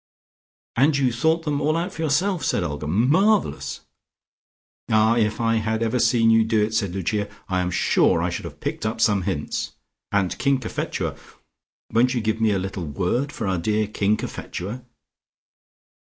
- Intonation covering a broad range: No, average, 4.6 semitones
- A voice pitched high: No, low, 110 Hz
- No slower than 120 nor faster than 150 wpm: No, average, 175 wpm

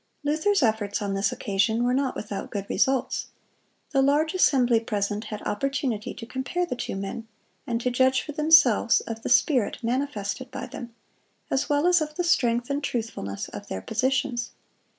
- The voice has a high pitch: Yes, high, 245 Hz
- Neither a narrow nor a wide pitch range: Yes, average, 4.3 semitones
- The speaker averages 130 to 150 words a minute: No, average, 170 wpm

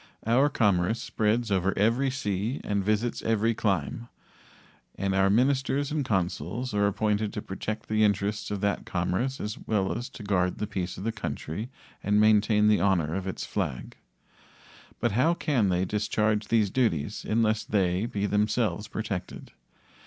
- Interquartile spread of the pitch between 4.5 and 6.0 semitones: No, average, 2.8 semitones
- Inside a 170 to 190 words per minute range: No, average, 160 wpm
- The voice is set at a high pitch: No, low, 105 Hz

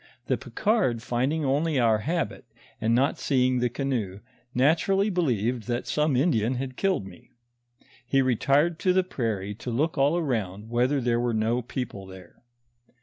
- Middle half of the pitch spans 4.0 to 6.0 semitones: Yes, average, 4.8 semitones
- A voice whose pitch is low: Yes, low, 125 Hz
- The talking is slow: No, average, 155 wpm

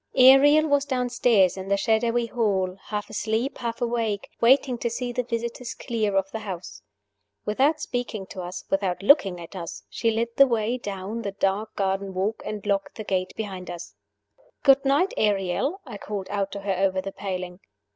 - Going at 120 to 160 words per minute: No, average, 180 wpm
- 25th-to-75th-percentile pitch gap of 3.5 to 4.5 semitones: Yes, average, 3.9 semitones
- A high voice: Yes, high, 210 Hz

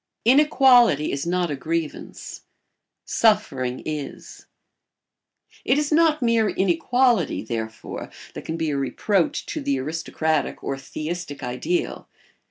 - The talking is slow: Yes, slow, 120 wpm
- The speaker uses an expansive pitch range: Yes, wide, 9.0 semitones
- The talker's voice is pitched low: No, medium, 165 Hz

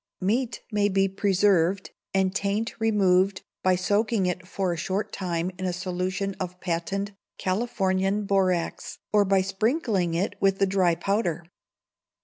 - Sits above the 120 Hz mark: Yes, high, 190 Hz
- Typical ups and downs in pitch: No, narrow, 1.8 semitones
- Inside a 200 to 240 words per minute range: No, average, 140 wpm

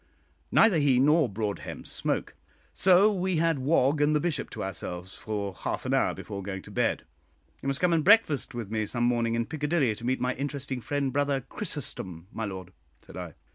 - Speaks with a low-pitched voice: Yes, low, 130 Hz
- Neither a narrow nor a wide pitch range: No, wide, 6.1 semitones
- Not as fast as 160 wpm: No, average, 195 wpm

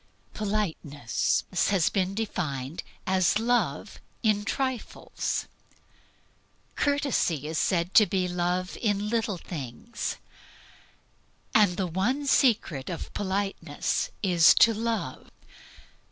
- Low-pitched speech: No, high, 190 Hz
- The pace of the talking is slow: Yes, slow, 95 wpm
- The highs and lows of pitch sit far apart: No, average, 4.3 semitones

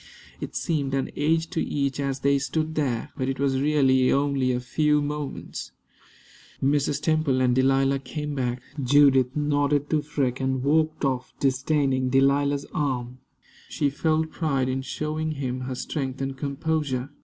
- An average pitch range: No, narrow, 2.2 semitones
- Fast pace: No, average, 155 wpm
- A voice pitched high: No, medium, 140 Hz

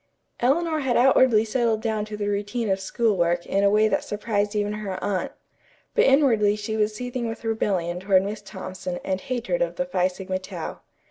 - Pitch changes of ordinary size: Yes, average, 3.4 semitones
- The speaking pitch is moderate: No, high, 210 Hz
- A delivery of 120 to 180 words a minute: No, average, 195 wpm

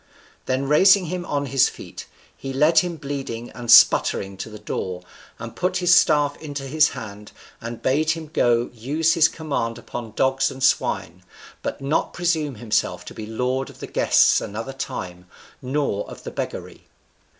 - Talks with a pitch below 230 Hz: Yes, low, 135 Hz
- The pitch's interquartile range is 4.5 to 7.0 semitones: Yes, average, 5.1 semitones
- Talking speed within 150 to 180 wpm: Yes, average, 170 wpm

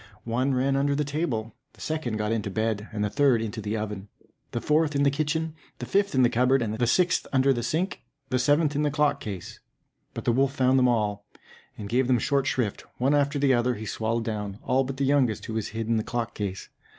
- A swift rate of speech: Yes, fast, 235 wpm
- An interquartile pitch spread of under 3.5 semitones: No, average, 4.2 semitones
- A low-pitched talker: Yes, low, 125 Hz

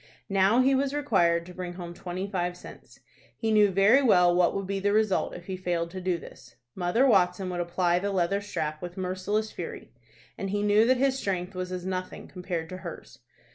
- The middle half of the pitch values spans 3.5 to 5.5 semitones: No, narrow, 2.5 semitones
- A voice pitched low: No, medium, 185 Hz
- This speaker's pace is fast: Yes, fast, 210 wpm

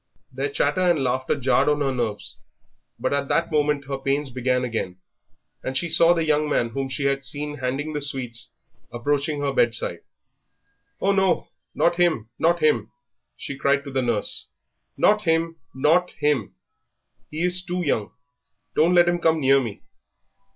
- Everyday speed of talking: Yes, average, 170 wpm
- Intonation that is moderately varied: Yes, average, 3.9 semitones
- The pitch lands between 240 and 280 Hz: No, medium, 140 Hz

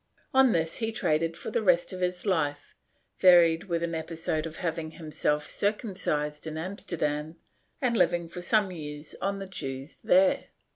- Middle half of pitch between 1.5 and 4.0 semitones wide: Yes, average, 3.1 semitones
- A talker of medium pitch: Yes, medium, 170 Hz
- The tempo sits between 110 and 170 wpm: Yes, average, 160 wpm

